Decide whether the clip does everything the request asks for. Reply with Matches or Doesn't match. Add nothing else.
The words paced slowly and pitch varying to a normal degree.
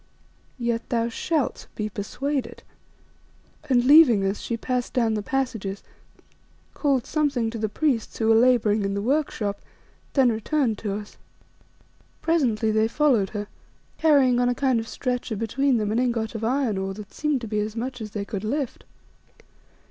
Doesn't match